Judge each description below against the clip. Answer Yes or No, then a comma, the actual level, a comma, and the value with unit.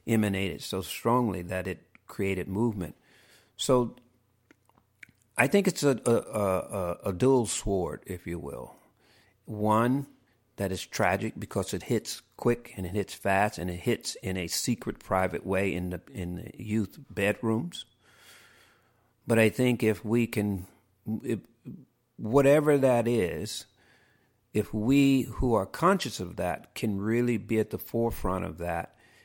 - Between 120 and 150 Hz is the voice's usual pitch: No, low, 110 Hz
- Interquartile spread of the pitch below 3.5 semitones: No, average, 4.3 semitones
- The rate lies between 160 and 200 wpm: No, average, 145 wpm